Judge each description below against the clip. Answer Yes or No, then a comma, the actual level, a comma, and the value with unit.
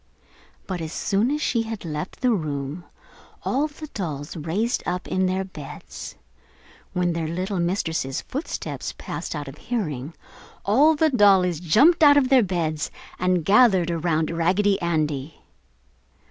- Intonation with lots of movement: Yes, wide, 5.8 semitones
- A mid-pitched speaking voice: Yes, medium, 180 Hz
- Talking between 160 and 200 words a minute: No, average, 145 wpm